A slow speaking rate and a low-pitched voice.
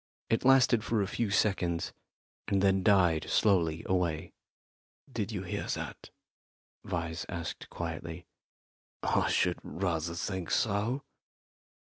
Yes: slow, 115 wpm; very low, 95 Hz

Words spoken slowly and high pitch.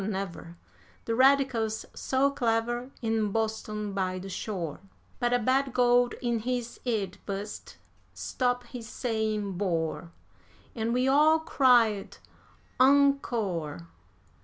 Yes: slow, 110 wpm; high, 225 Hz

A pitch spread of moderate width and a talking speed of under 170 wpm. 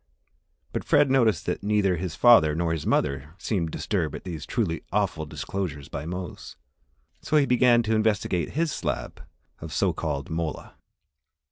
No: wide, 6.2 semitones; average, 150 wpm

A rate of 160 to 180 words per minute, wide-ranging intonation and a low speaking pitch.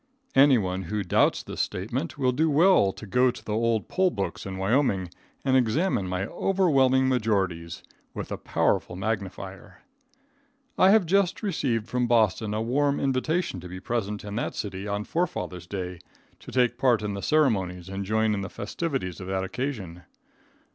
Yes: average, 170 wpm; wide, 5.8 semitones; low, 110 Hz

